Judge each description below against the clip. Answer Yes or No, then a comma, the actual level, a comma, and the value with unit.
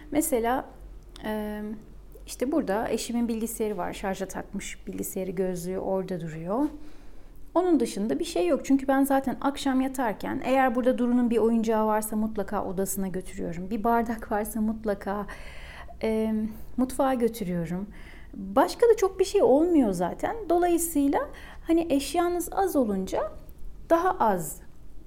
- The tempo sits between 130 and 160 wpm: No, average, 120 wpm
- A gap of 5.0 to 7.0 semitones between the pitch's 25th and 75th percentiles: Yes, wide, 5.5 semitones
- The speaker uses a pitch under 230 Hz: No, high, 235 Hz